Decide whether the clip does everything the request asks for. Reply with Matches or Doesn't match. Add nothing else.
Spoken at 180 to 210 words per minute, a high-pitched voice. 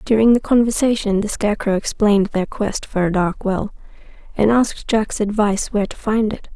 Matches